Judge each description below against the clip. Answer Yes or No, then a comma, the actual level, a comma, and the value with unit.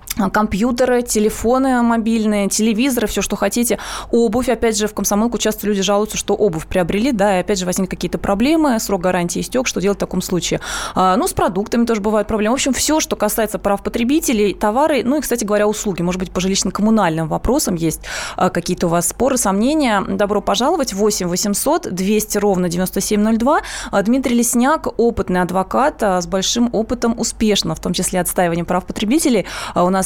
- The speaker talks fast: Yes, fast, 170 wpm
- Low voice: No, high, 210 Hz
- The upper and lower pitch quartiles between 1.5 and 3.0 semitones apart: No, average, 3.8 semitones